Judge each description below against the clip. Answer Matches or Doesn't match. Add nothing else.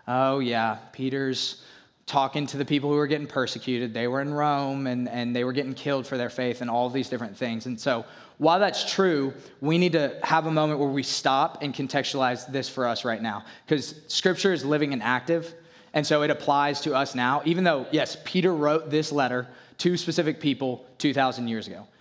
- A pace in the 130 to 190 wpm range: Doesn't match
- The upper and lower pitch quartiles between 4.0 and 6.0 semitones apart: Doesn't match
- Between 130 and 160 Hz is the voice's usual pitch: Matches